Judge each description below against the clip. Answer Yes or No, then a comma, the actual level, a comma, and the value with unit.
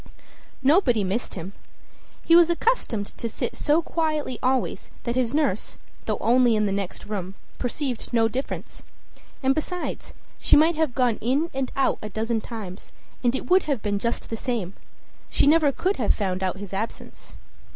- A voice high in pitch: Yes, high, 245 Hz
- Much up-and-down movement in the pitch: Yes, wide, 5.7 semitones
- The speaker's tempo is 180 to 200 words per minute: No, average, 170 wpm